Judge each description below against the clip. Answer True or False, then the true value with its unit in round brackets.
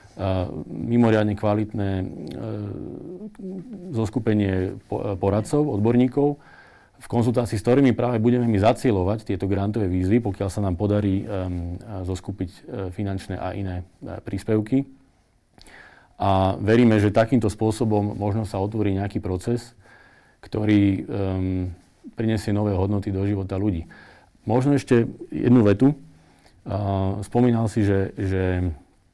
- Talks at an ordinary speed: True (120 wpm)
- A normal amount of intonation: True (3.5 semitones)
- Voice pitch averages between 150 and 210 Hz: False (105 Hz)